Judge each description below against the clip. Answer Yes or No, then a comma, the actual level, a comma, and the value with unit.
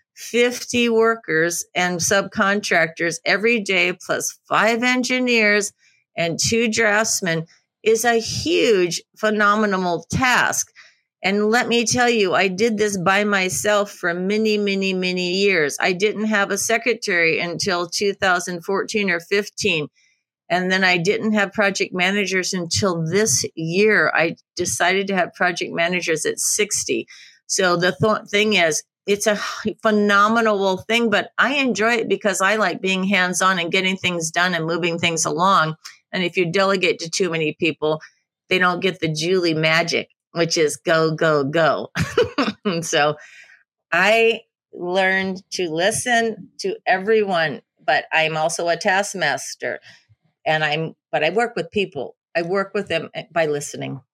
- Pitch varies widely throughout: No, average, 3.8 semitones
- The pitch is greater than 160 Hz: Yes, high, 190 Hz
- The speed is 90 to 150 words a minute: Yes, average, 145 wpm